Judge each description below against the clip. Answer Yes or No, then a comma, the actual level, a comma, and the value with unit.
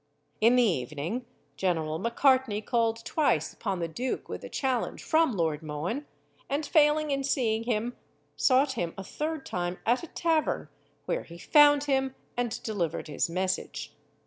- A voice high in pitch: Yes, high, 235 Hz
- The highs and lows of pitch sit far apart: Yes, wide, 7.4 semitones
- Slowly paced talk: No, average, 155 wpm